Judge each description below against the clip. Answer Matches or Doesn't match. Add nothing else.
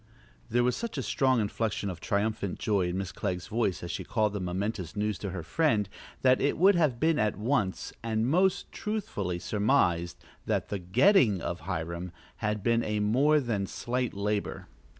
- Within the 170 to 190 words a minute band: Matches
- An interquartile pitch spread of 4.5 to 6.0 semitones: Matches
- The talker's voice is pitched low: Matches